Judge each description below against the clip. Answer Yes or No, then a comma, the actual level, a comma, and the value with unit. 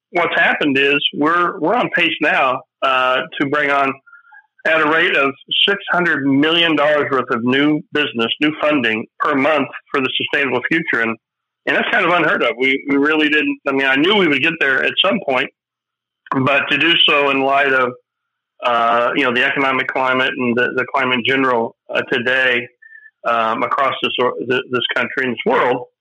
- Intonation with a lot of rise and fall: No, average, 2.9 semitones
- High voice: No, medium, 140 Hz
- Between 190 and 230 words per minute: Yes, average, 195 wpm